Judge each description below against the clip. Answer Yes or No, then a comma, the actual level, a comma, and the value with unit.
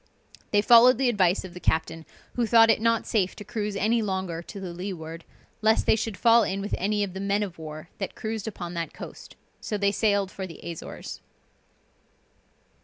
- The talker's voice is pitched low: No, high, 200 Hz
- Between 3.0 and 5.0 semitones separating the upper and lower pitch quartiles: Yes, average, 3.5 semitones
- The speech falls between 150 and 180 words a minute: No, average, 195 wpm